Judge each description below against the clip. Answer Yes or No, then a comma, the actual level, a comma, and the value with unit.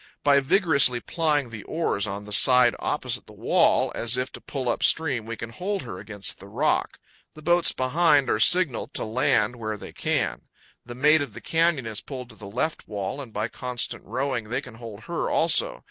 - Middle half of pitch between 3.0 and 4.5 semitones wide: No, average, 5.1 semitones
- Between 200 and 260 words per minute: Yes, fast, 205 wpm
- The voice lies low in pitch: Yes, low, 125 Hz